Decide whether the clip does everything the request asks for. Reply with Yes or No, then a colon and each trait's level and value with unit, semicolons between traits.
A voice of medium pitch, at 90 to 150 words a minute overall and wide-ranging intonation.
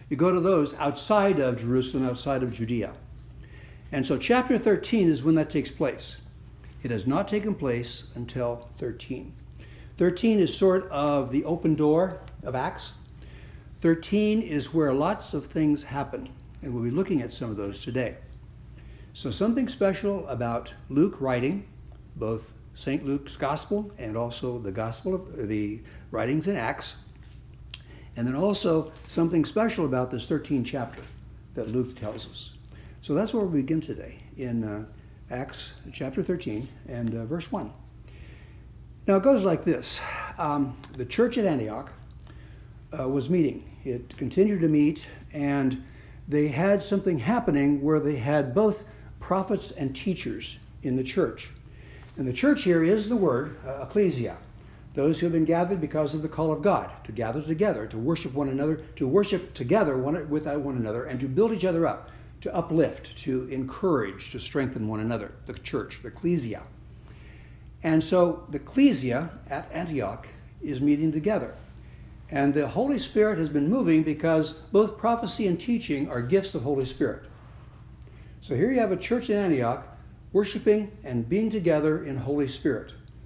No: medium, 145 Hz; average, 160 wpm; wide, 6.6 semitones